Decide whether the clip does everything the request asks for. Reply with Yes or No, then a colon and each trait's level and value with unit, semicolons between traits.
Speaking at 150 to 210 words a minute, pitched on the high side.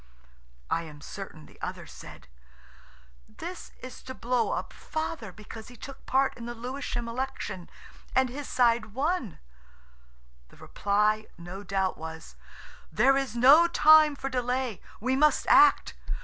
No: average, 140 wpm; high, 245 Hz